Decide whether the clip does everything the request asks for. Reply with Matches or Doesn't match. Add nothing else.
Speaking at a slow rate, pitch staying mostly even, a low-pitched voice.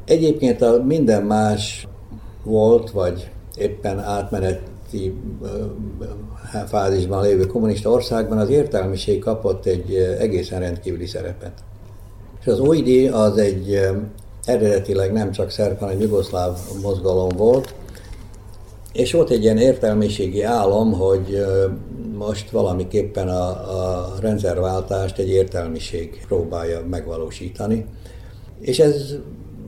Matches